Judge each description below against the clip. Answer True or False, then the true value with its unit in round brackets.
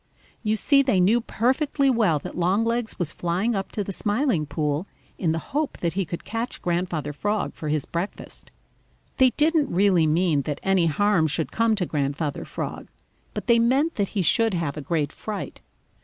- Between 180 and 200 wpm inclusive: True (185 wpm)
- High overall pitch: True (195 Hz)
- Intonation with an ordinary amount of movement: False (6.0 semitones)